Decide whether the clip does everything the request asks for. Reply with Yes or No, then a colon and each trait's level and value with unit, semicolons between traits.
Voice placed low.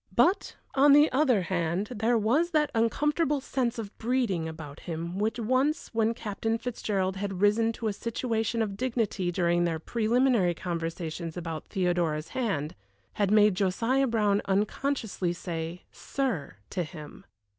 No: high, 210 Hz